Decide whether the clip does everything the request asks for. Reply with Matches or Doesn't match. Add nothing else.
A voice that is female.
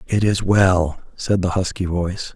Doesn't match